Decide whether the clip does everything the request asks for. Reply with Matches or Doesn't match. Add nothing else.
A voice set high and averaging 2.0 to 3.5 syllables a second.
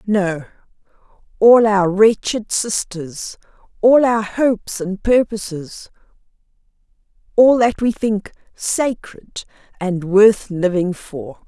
Matches